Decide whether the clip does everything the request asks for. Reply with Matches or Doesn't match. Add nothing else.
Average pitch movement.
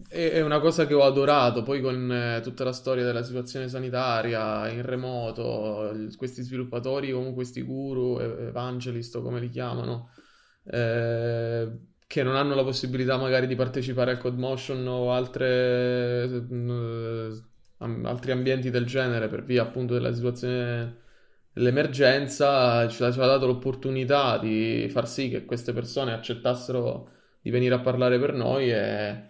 Doesn't match